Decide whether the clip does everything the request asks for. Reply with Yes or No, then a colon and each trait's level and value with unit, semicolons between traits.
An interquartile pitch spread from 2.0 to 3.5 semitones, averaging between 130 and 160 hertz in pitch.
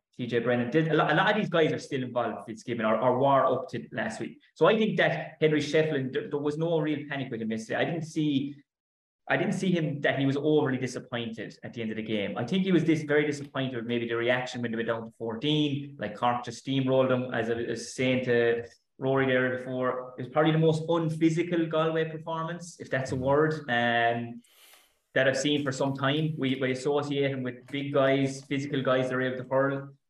No: average, 4.0 semitones; low, 135 Hz